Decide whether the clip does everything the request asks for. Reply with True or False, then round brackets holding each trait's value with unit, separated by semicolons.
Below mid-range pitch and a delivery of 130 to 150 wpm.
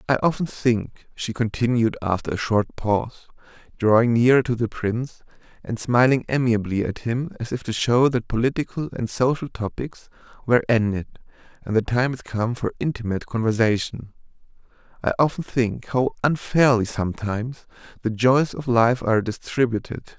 True (120 Hz; 145 wpm)